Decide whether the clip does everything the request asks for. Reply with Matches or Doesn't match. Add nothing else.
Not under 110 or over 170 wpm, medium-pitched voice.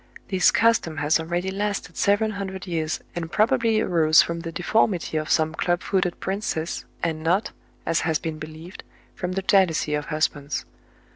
Matches